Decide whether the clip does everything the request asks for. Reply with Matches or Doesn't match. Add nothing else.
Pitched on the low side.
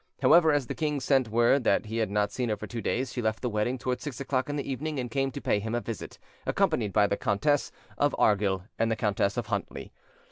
Matches